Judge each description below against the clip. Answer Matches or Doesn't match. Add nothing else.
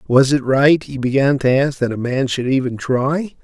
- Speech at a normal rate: Doesn't match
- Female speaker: Doesn't match